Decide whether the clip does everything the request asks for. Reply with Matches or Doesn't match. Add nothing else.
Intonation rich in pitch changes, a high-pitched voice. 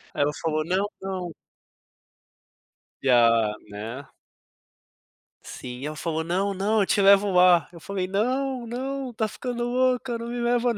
Matches